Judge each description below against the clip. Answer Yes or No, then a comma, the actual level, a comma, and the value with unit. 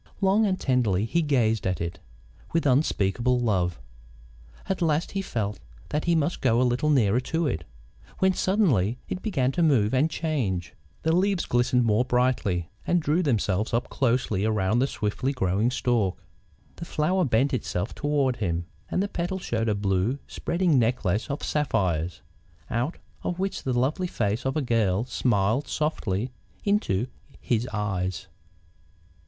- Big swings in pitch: Yes, wide, 6.7 semitones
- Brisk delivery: No, average, 155 wpm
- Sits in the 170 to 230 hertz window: No, low, 125 Hz